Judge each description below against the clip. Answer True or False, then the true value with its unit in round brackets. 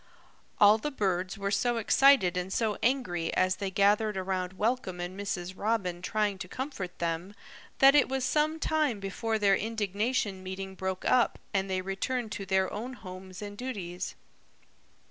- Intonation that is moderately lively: True (3.6 semitones)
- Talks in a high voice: True (200 Hz)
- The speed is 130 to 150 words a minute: False (165 wpm)